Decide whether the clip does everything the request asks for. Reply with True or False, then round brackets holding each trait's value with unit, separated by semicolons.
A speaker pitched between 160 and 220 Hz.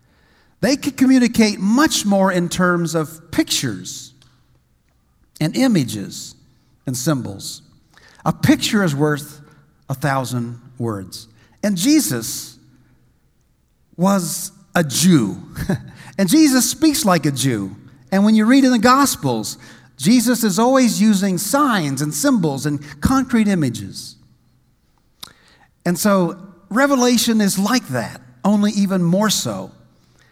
True (185 Hz)